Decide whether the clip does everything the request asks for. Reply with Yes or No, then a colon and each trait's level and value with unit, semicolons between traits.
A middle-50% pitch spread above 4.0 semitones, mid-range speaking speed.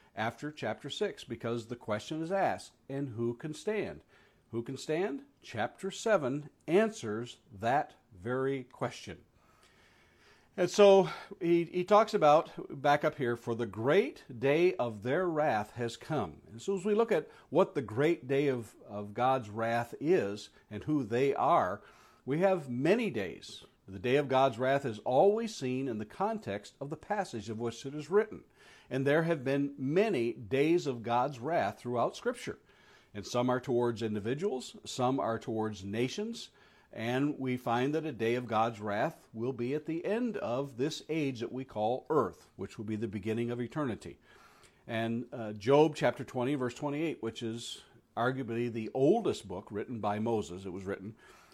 Yes: average, 4.9 semitones; average, 170 wpm